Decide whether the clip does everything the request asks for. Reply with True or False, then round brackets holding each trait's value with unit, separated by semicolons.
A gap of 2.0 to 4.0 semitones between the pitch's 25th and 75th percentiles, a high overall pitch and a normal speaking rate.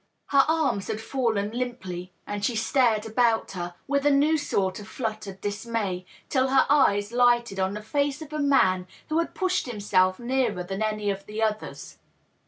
False (5.0 semitones; 220 Hz; 180 wpm)